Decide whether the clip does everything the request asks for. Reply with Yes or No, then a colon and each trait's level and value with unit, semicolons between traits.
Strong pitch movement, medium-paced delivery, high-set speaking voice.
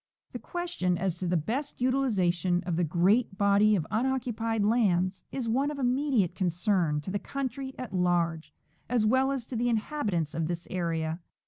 Yes: wide, 6.2 semitones; average, 175 wpm; high, 205 Hz